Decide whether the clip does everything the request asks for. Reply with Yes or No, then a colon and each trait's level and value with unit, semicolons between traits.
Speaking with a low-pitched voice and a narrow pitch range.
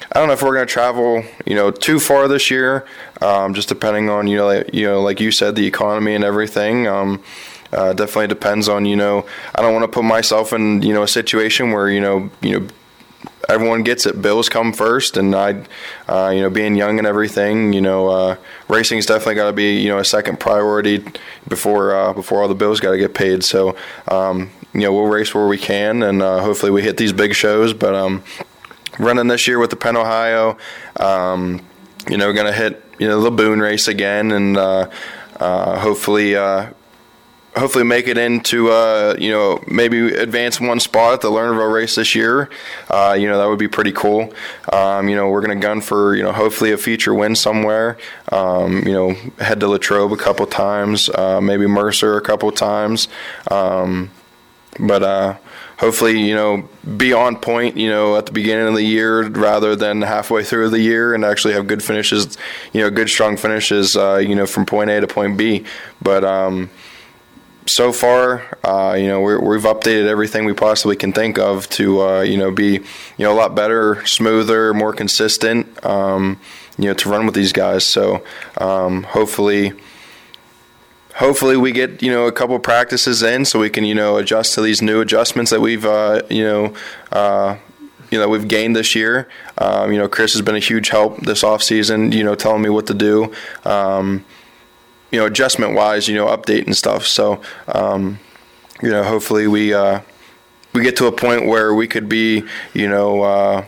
Yes: low, 105 Hz; narrow, 1.9 semitones